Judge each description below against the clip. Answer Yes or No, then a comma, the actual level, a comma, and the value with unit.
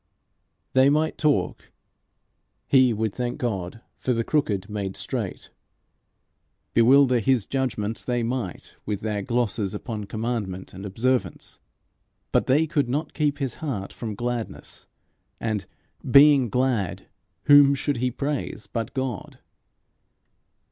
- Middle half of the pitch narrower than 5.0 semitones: Yes, average, 4.2 semitones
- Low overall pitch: Yes, low, 120 Hz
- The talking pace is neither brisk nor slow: No, slow, 120 wpm